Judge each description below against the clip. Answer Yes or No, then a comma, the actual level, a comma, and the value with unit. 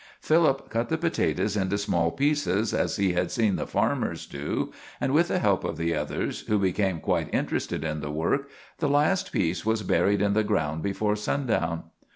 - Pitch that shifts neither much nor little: No, wide, 7.4 semitones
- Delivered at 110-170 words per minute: No, average, 190 wpm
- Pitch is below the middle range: Yes, low, 105 Hz